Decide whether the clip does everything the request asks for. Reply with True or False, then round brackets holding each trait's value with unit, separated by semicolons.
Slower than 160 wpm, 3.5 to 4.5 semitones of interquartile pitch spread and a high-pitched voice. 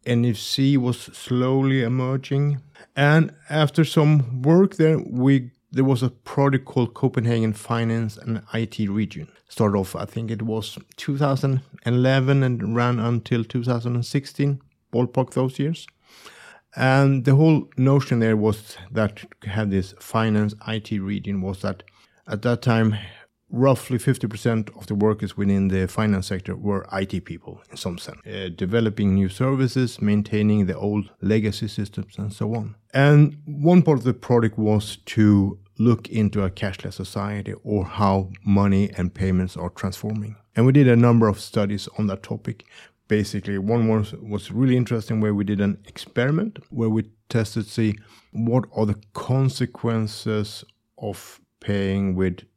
False (150 wpm; 3.9 semitones; 110 Hz)